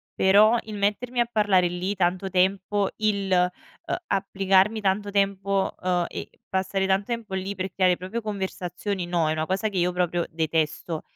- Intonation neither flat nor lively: No, narrow, 2.1 semitones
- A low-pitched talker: No, high, 190 Hz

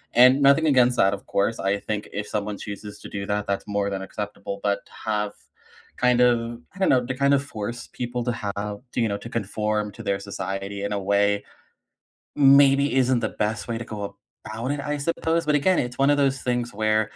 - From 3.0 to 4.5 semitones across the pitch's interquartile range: Yes, average, 4.1 semitones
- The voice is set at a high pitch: No, low, 110 Hz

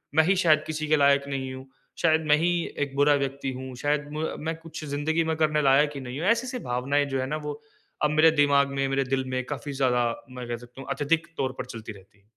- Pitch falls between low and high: Yes, medium, 145 Hz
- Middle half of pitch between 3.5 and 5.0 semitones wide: No, average, 2.8 semitones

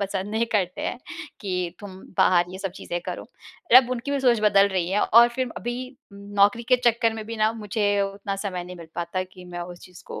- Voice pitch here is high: Yes, high, 200 Hz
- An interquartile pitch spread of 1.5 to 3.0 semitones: No, average, 3.8 semitones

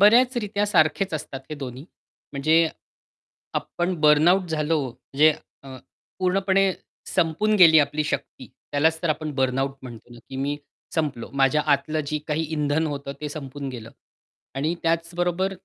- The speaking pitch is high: No, medium, 155 Hz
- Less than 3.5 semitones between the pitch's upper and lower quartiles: No, average, 3.8 semitones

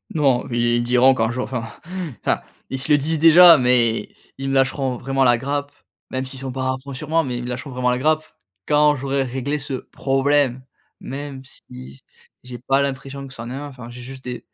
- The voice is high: No, low, 135 Hz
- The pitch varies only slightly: Yes, narrow, 2.2 semitones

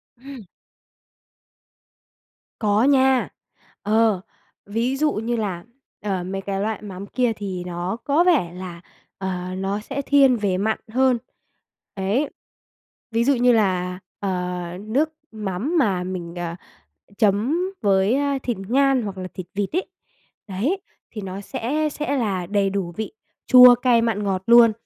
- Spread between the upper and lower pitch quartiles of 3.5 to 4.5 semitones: No, average, 4.9 semitones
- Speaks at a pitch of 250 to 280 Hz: No, high, 210 Hz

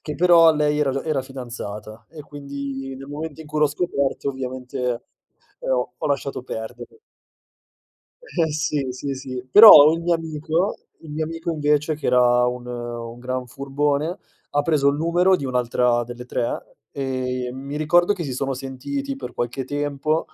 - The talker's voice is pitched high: No, medium, 140 Hz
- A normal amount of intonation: Yes, average, 3.3 semitones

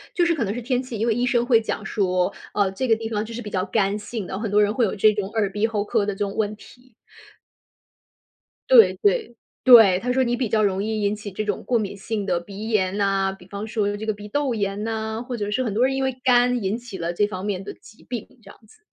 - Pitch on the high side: Yes, high, 215 Hz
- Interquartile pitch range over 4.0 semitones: No, average, 3.0 semitones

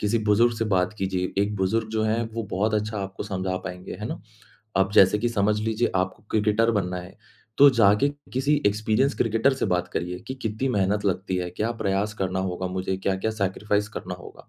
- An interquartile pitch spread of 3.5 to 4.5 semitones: No, average, 2.8 semitones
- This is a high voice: No, low, 105 Hz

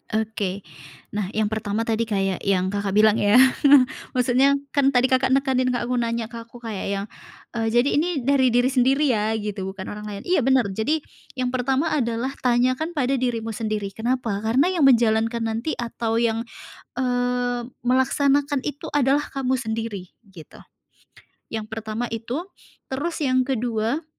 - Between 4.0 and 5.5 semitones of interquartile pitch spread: No, average, 3.1 semitones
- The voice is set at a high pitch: Yes, high, 235 Hz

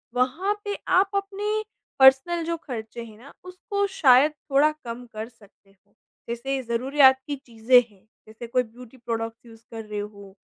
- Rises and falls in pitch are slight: No, average, 4.3 semitones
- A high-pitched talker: Yes, very high, 250 Hz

